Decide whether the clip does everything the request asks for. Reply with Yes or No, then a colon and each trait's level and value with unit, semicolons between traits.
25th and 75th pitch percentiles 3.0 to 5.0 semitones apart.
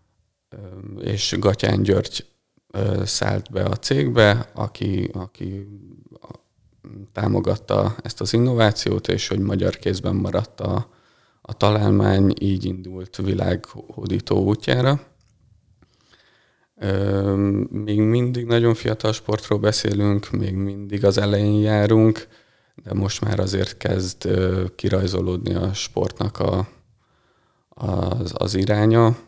No: narrow, 2.4 semitones